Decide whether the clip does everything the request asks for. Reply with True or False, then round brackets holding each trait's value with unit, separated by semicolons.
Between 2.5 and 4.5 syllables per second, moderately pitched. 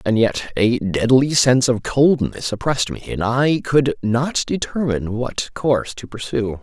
False (4.4 syllables/s; 125 Hz)